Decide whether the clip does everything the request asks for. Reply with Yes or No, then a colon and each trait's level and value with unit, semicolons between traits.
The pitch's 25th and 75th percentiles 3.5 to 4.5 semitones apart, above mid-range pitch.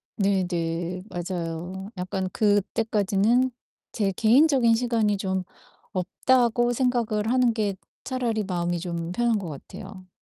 Yes: average, 4.2 semitones; high, 200 Hz